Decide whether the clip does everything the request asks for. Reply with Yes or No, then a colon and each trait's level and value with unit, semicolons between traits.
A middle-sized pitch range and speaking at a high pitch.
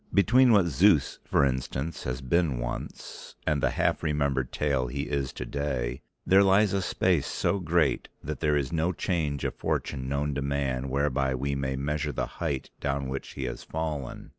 No: average, 3.2 semitones; very low, 70 Hz